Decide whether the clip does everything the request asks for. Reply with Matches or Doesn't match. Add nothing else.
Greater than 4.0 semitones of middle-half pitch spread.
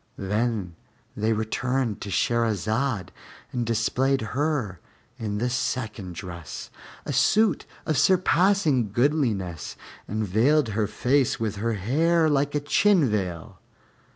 Matches